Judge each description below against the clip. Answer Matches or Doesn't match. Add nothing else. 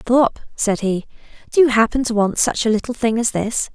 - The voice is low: Doesn't match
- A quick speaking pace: Matches